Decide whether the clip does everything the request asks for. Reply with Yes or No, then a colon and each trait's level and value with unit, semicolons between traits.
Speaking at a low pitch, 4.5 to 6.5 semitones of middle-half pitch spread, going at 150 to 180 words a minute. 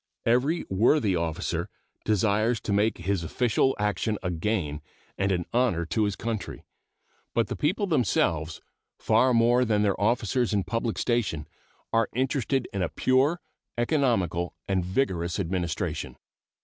No: low, 110 Hz; average, 5.0 semitones; slow, 135 wpm